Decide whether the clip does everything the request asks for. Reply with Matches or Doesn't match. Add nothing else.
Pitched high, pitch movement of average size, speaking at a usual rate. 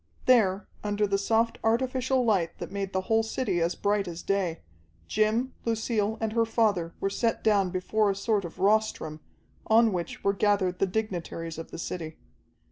Matches